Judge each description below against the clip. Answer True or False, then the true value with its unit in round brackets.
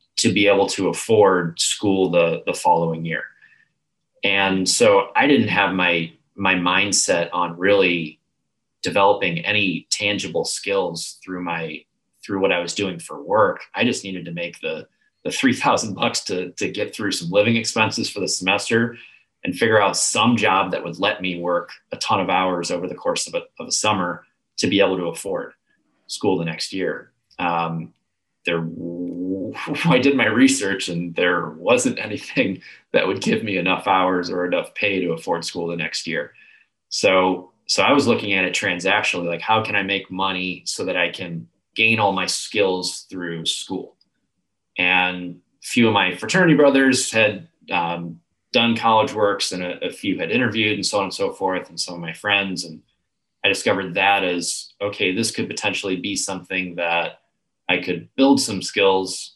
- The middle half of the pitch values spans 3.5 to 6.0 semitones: False (2.9 semitones)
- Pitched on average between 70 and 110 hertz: True (95 Hz)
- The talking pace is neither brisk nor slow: True (180 wpm)